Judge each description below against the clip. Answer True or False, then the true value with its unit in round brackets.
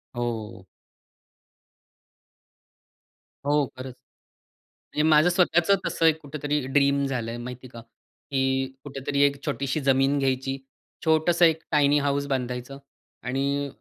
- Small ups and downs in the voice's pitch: True (1.9 semitones)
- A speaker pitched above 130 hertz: True (140 Hz)